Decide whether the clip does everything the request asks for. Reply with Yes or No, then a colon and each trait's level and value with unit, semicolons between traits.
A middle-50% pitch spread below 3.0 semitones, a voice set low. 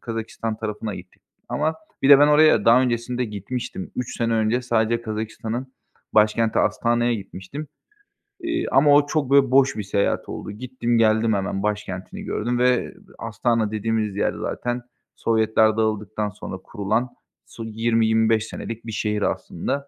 Yes: narrow, 2.6 semitones; low, 115 Hz